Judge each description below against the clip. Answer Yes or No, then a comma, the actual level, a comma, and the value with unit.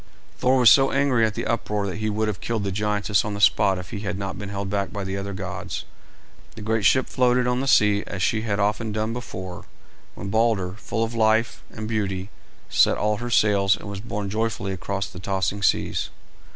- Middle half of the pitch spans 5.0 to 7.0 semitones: No, narrow, 2.4 semitones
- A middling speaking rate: No, fast, 215 wpm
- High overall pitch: No, low, 105 Hz